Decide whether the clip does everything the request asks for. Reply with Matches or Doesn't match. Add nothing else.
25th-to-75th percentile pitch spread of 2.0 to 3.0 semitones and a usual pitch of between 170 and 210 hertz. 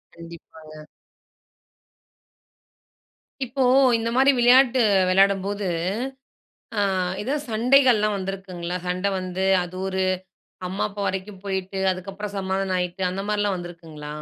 Matches